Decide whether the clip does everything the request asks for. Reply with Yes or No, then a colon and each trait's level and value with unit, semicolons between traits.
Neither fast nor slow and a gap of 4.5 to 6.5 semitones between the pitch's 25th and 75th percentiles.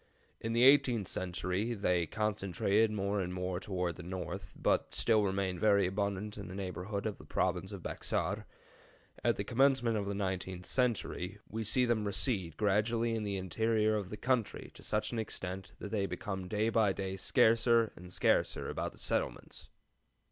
No: average, 175 wpm; average, 3.1 semitones